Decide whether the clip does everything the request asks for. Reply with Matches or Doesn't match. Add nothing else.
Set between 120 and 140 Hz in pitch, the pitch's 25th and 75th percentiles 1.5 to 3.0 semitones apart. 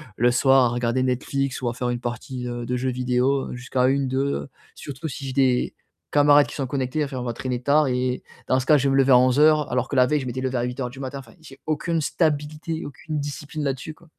Matches